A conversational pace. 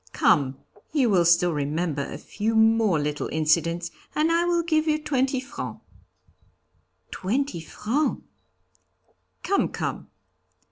No: slow, 120 wpm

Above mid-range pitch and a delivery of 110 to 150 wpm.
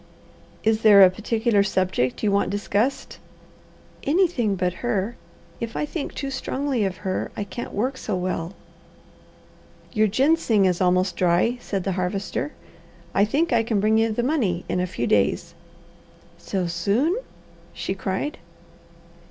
Yes: high, 205 Hz; average, 145 wpm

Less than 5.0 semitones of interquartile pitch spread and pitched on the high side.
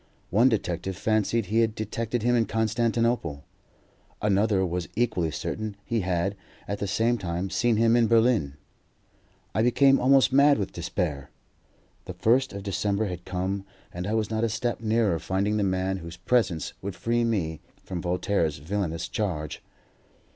No: average, 4.1 semitones; low, 105 Hz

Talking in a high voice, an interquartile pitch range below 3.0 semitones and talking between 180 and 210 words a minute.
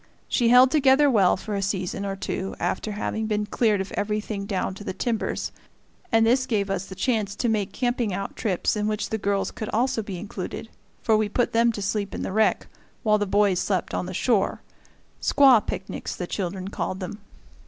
Yes: high, 210 Hz; narrow, 2.5 semitones; fast, 205 wpm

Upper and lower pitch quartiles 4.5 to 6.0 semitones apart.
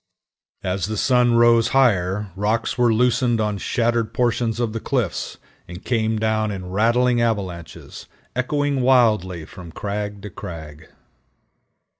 No: average, 3.6 semitones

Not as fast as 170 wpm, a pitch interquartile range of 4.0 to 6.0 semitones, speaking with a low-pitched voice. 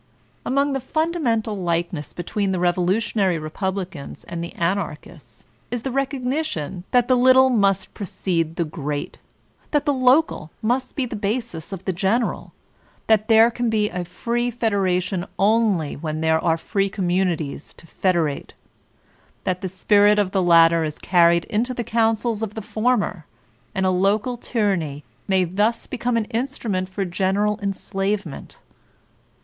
No: average, 155 wpm; average, 4.9 semitones; high, 195 Hz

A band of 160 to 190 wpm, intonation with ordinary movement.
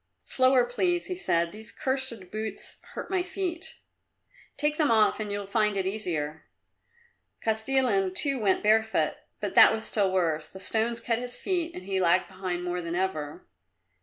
No: average, 165 wpm; wide, 5.7 semitones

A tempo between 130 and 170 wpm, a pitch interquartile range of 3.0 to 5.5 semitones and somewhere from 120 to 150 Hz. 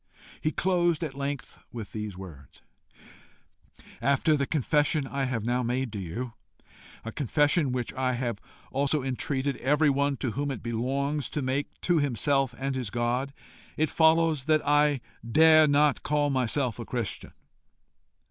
Yes: average, 150 wpm; average, 3.3 semitones; low, 135 Hz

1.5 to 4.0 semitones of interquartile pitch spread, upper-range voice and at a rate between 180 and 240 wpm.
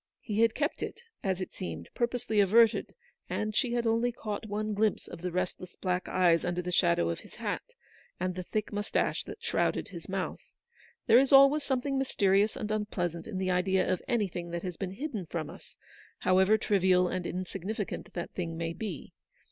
Yes: average, 3.5 semitones; high, 195 Hz; average, 190 wpm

